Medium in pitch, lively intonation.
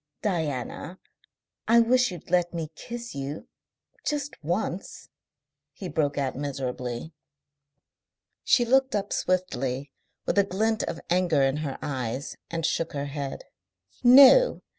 Yes: medium, 165 Hz; wide, 7.6 semitones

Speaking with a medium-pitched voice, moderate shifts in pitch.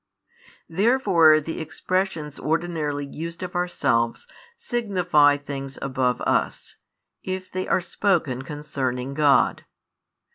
Yes: medium, 155 Hz; average, 4.4 semitones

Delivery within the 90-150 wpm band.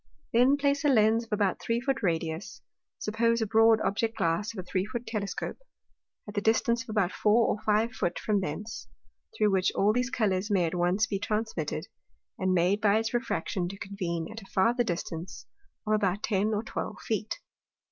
No: average, 190 wpm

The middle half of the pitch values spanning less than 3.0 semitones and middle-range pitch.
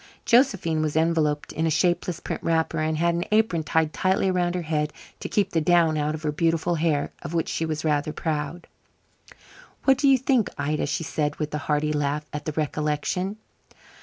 Yes: narrow, 2.5 semitones; medium, 160 Hz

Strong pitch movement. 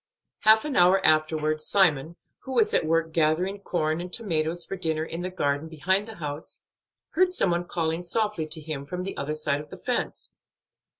No: average, 3.5 semitones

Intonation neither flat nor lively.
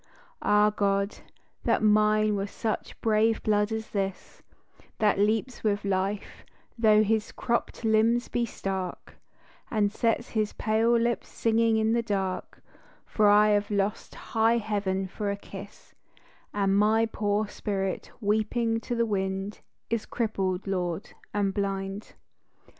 No: narrow, 1.9 semitones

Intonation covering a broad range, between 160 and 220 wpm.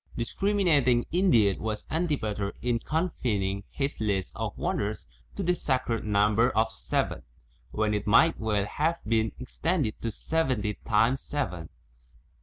No: wide, 6.0 semitones; slow, 135 wpm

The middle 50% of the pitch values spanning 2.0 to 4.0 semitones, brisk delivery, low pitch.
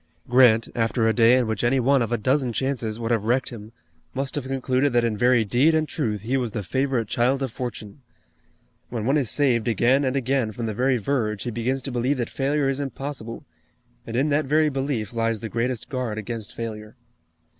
Yes: average, 3.0 semitones; fast, 210 wpm; low, 125 Hz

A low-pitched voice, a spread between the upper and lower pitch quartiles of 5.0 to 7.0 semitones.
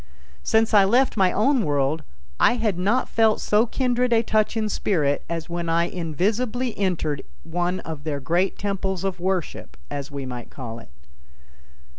No: medium, 185 Hz; wide, 5.5 semitones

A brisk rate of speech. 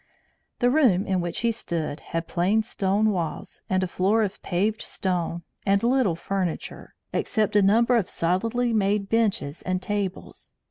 No: average, 155 wpm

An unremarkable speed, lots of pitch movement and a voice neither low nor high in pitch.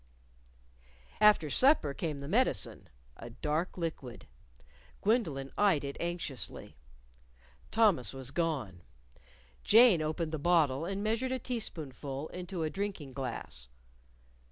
No: slow, 115 wpm; wide, 6.2 semitones; medium, 160 Hz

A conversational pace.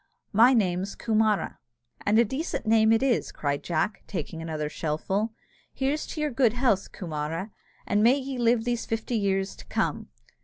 Yes: average, 175 wpm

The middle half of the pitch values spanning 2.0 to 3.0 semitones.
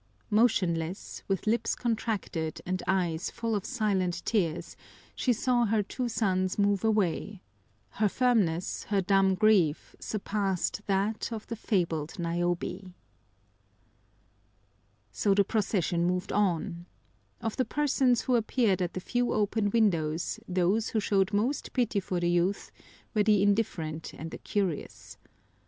No: average, 3.7 semitones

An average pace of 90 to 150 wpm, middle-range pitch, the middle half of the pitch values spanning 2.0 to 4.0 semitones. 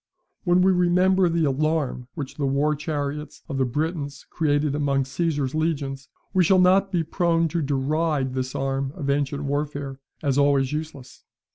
No: average, 160 wpm; medium, 145 Hz; average, 3.2 semitones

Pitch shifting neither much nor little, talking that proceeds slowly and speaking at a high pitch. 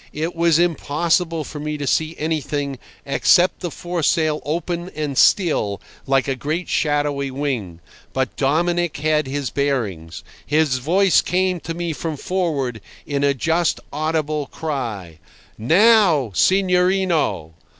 No: average, 3.9 semitones; slow, 130 wpm; medium, 155 Hz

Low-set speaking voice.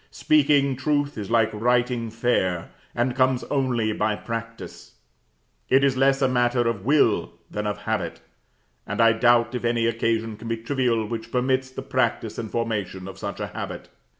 Yes: low, 120 Hz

